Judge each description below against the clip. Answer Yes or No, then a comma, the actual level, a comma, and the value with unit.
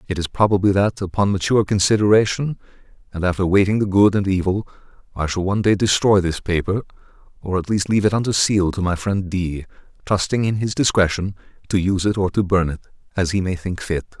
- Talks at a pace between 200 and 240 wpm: Yes, fast, 205 wpm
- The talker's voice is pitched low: Yes, very low, 95 Hz